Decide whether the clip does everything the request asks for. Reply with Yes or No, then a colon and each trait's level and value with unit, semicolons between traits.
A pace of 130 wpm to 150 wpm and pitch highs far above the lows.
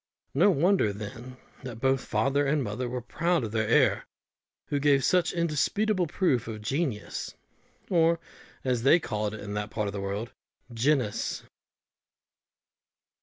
Yes: average, 145 wpm; wide, 6.1 semitones